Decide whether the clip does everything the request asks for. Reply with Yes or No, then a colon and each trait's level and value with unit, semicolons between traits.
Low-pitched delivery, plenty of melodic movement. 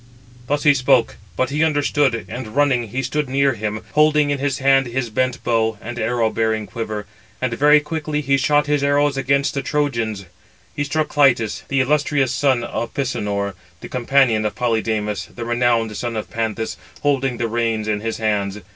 No: low, 125 Hz; average, 4.0 semitones